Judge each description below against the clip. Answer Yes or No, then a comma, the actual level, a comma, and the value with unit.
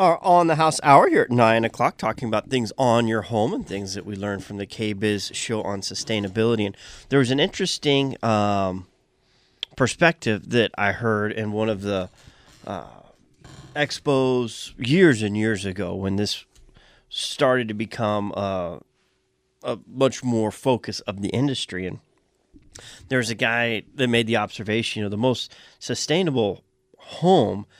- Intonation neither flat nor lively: Yes, average, 3.9 semitones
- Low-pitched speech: Yes, low, 110 Hz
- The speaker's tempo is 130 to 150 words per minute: No, average, 160 wpm